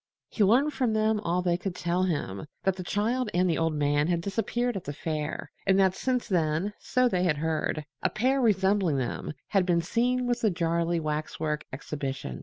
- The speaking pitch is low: No, medium, 180 Hz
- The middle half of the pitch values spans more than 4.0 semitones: Yes, wide, 5.5 semitones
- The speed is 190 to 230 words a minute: Yes, average, 200 wpm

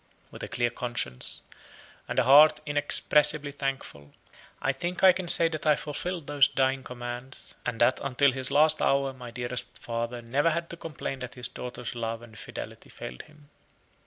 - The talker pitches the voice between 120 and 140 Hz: Yes, low, 135 Hz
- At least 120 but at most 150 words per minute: No, average, 175 wpm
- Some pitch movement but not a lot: Yes, average, 3.6 semitones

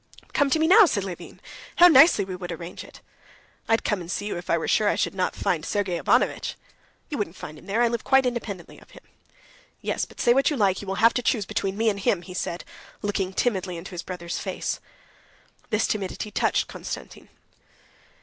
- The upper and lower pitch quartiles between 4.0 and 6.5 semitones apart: Yes, average, 4.4 semitones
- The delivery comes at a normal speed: No, fast, 215 wpm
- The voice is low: No, high, 200 Hz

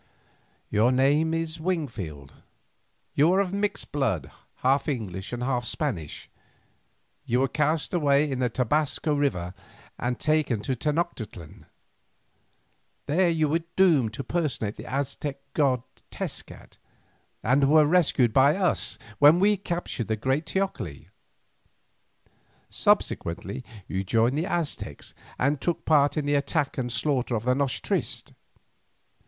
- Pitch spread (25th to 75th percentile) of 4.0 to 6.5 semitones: Yes, average, 4.5 semitones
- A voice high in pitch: No, medium, 140 Hz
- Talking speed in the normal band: No, slow, 130 wpm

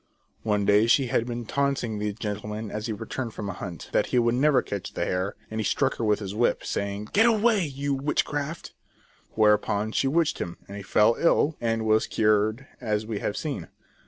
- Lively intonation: No, average, 4.5 semitones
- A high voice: No, low, 110 Hz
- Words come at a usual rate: No, fast, 210 wpm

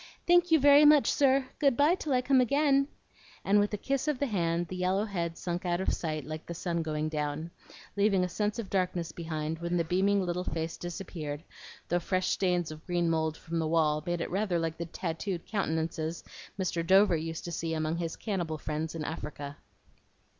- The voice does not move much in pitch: No, average, 3.9 semitones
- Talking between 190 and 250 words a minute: Yes, fast, 205 wpm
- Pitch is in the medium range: Yes, medium, 175 Hz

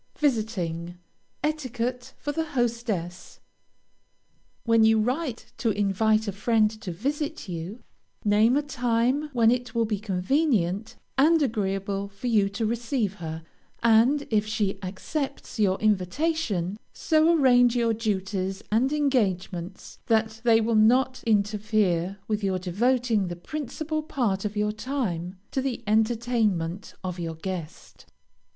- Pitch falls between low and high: No, high, 220 Hz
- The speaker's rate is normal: No, slow, 130 wpm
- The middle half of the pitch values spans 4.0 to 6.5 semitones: Yes, average, 4.3 semitones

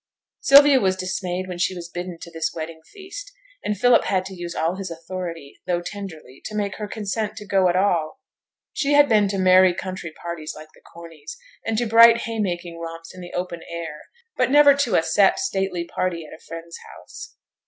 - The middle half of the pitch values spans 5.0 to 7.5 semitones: No, average, 4.0 semitones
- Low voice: No, medium, 185 Hz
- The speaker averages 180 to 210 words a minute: Yes, average, 200 wpm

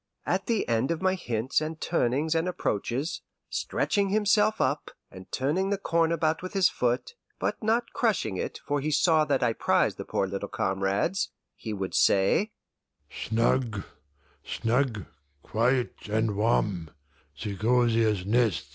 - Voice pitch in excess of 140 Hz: No, low, 135 Hz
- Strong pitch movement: Yes, wide, 8.1 semitones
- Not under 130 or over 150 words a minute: Yes, average, 140 wpm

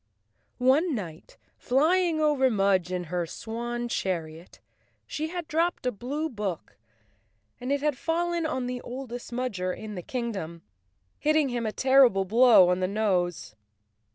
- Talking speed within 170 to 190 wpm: No, average, 145 wpm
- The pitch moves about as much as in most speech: No, wide, 7.1 semitones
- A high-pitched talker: Yes, high, 240 Hz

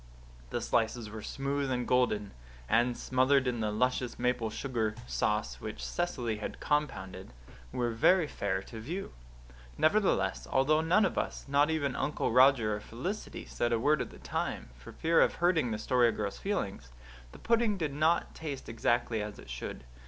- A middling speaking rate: Yes, average, 170 wpm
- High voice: No, low, 125 Hz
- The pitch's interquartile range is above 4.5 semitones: Yes, wide, 5.5 semitones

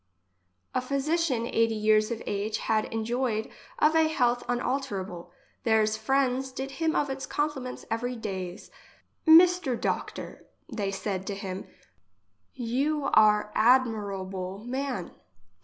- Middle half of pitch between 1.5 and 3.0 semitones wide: No, average, 4.2 semitones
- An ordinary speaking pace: No, slow, 125 wpm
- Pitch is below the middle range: No, high, 235 Hz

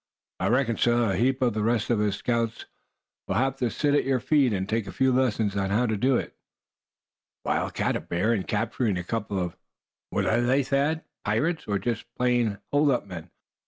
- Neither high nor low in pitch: No, low, 115 Hz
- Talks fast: Yes, fast, 210 wpm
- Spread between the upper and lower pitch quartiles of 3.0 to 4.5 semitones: Yes, average, 3.9 semitones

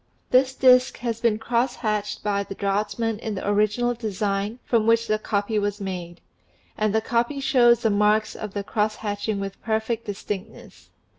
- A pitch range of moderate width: No, narrow, 2.3 semitones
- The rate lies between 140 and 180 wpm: Yes, average, 170 wpm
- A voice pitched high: Yes, high, 215 Hz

